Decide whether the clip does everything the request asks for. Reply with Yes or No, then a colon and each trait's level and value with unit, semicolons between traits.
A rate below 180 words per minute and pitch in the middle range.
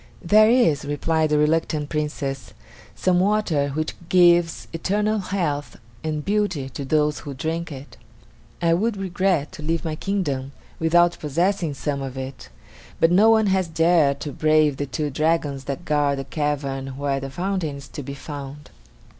Yes: average, 165 wpm; medium, 155 Hz